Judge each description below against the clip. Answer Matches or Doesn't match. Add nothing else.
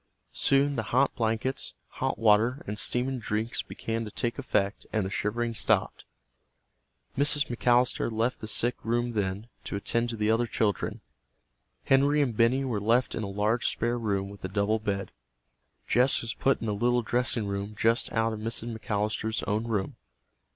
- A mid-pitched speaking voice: Doesn't match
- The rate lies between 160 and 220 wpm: Matches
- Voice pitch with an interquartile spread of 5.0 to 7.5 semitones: Doesn't match